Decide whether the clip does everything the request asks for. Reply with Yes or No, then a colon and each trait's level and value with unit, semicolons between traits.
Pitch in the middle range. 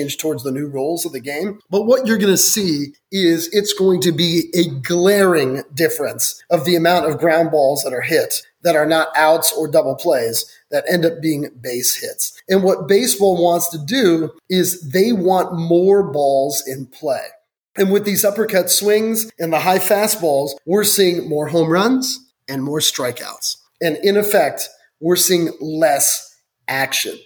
Yes: medium, 175 Hz